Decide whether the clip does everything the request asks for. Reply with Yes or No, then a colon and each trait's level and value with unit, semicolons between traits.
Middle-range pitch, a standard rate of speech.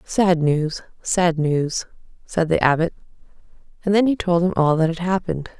Yes: medium, 170 Hz; average, 170 wpm